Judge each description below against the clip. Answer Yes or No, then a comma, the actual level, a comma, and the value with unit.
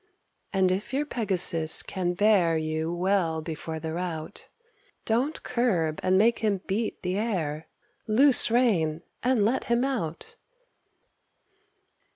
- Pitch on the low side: No, high, 190 Hz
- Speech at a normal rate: No, slow, 125 wpm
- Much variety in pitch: Yes, wide, 6.0 semitones